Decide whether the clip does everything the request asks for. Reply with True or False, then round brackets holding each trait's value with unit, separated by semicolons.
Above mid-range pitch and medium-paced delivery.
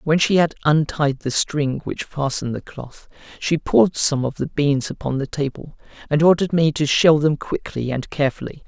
False (145 Hz; 195 wpm)